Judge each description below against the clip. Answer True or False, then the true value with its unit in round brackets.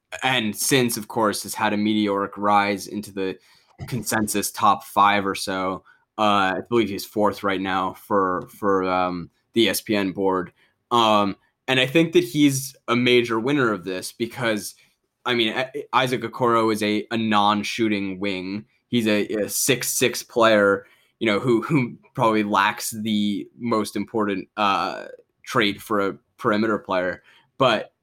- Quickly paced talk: False (150 wpm)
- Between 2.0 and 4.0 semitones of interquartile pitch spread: True (2.8 semitones)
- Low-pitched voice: True (105 Hz)